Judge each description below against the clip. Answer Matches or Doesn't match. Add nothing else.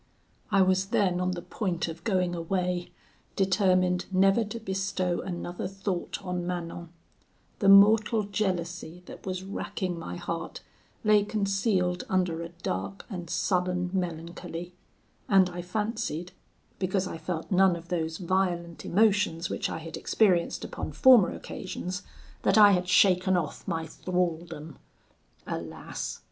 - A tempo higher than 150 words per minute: Doesn't match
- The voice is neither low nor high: Matches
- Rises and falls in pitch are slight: Matches